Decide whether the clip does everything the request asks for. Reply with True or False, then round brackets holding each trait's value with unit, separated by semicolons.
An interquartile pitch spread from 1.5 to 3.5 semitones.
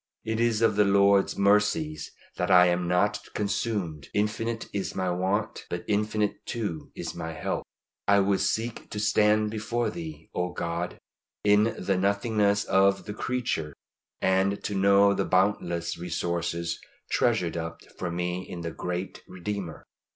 True (3.1 semitones)